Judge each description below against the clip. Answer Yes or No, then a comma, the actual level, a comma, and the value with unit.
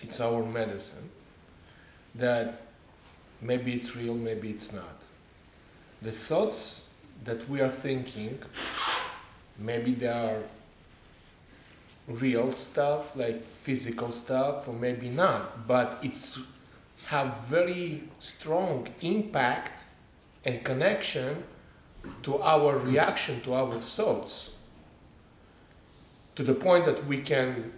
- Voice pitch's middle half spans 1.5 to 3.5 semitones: Yes, average, 3.1 semitones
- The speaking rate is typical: No, slow, 100 wpm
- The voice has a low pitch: Yes, low, 120 Hz